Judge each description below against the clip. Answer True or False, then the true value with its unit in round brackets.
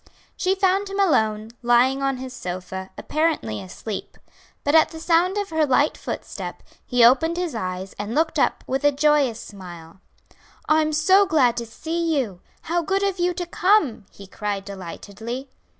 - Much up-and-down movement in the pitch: True (7.7 semitones)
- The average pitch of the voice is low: False (275 Hz)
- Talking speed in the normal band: True (165 wpm)